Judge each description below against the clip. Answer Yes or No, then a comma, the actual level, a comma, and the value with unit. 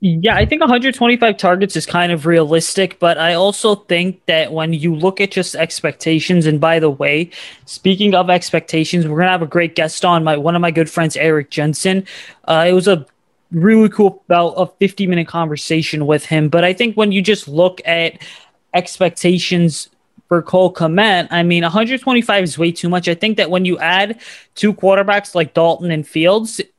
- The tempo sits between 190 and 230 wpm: Yes, average, 195 wpm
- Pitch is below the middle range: No, medium, 175 Hz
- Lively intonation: No, average, 2.9 semitones